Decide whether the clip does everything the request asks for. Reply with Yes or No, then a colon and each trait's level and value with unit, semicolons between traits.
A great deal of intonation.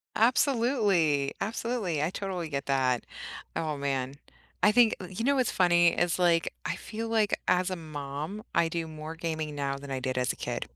Yes: wide, 6.4 semitones